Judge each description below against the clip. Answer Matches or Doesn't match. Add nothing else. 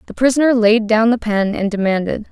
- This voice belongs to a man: Doesn't match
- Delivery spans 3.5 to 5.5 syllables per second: Doesn't match